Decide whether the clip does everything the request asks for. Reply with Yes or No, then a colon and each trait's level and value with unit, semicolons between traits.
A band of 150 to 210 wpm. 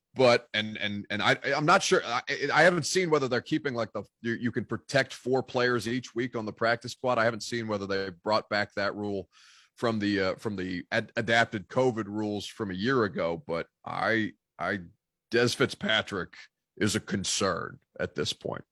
Yes: average, 200 wpm